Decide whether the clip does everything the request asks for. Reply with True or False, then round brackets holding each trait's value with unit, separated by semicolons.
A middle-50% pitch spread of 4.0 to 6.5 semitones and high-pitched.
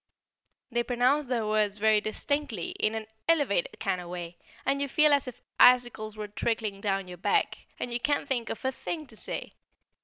True (4.7 semitones; 235 Hz)